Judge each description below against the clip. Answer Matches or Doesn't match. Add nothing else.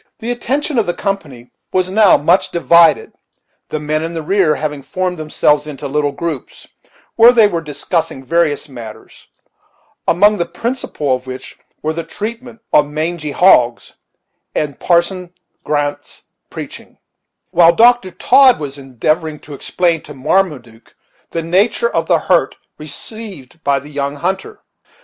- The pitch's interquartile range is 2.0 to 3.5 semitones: Doesn't match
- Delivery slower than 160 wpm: Matches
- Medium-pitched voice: Matches